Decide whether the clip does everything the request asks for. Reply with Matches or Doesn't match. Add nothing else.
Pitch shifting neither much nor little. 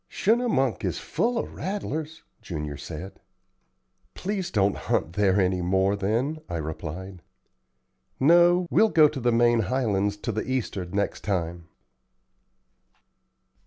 Doesn't match